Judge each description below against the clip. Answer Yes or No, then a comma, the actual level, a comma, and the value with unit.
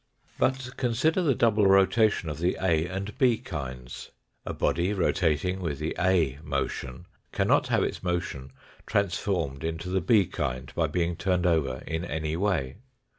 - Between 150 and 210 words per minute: Yes, average, 155 wpm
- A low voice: Yes, very low, 90 Hz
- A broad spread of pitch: No, average, 4.3 semitones